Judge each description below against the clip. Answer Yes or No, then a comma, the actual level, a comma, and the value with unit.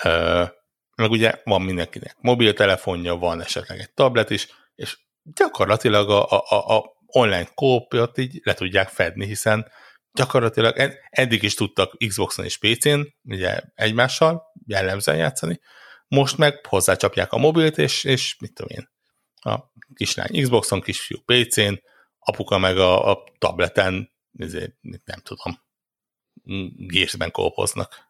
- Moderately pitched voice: No, low, 110 Hz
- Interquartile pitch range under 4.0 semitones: No, average, 5.3 semitones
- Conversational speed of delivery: Yes, average, 125 wpm